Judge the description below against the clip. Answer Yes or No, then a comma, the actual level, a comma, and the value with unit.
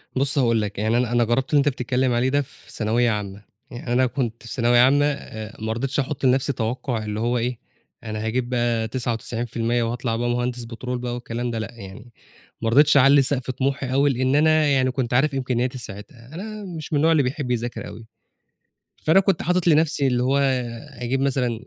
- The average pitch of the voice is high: No, low, 125 Hz